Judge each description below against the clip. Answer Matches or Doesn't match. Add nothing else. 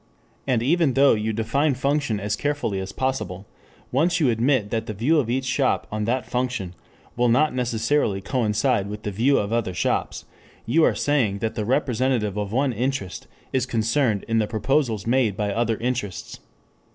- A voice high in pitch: Doesn't match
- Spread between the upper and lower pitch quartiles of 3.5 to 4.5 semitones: Matches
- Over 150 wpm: Matches